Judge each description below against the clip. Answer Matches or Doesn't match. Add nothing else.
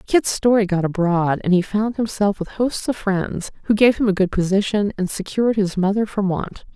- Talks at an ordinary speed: Doesn't match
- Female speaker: Matches